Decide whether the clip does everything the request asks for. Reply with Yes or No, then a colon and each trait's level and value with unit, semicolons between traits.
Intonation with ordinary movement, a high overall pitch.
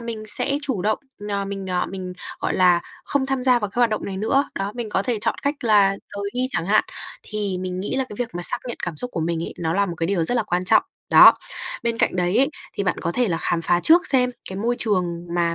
Yes: average, 4.9 semitones; high, 200 Hz